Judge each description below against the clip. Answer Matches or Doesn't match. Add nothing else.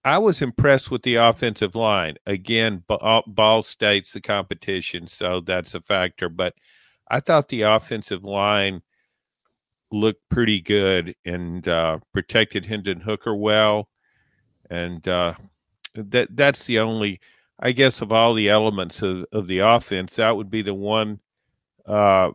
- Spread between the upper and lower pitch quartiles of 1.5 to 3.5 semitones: Matches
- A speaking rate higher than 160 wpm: Doesn't match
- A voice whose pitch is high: Doesn't match